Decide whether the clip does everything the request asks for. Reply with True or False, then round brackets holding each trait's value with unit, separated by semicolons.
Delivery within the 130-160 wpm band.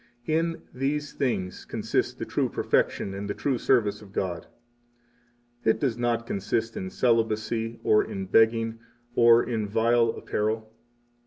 True (140 wpm)